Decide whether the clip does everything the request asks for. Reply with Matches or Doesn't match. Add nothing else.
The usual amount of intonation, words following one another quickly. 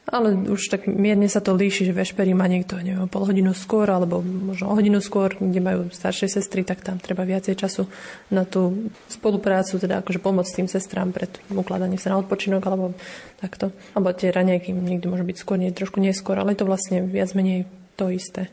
Doesn't match